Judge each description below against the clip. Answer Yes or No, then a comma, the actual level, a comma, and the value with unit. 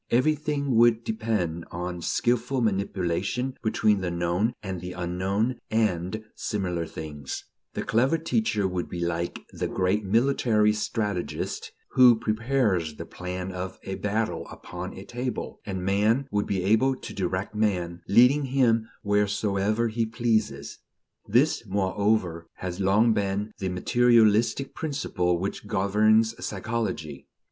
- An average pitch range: Yes, average, 4.1 semitones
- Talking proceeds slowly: Yes, slow, 130 wpm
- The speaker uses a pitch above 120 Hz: No, low, 105 Hz